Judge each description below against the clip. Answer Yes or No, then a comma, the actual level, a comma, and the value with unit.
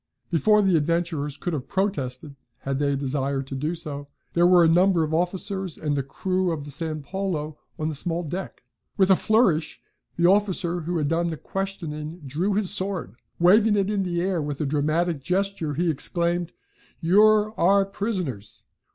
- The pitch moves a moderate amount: Yes, average, 4.2 semitones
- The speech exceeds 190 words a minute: No, average, 180 wpm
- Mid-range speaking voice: Yes, medium, 170 Hz